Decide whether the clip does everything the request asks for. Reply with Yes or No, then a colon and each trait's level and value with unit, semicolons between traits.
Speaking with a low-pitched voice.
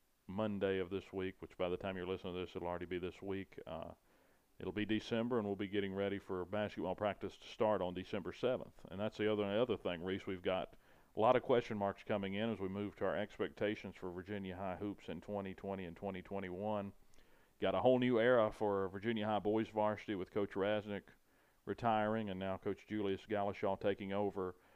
Yes: low, 100 Hz